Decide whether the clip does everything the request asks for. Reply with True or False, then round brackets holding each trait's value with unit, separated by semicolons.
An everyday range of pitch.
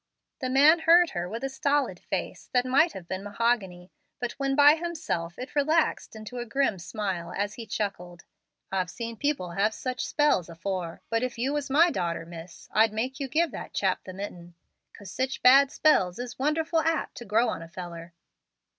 False (7.2 semitones)